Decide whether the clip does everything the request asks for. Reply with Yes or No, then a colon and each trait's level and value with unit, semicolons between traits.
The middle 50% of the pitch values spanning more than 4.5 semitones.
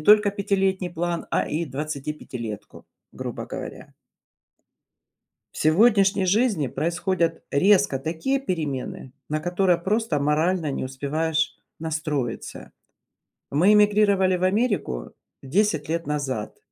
Yes: average, 4.9 semitones